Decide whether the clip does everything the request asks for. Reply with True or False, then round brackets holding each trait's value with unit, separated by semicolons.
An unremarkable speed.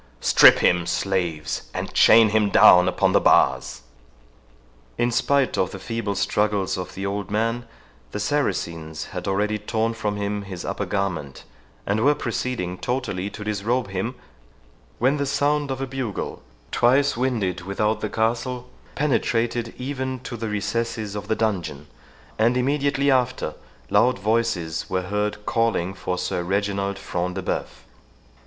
True (150 wpm)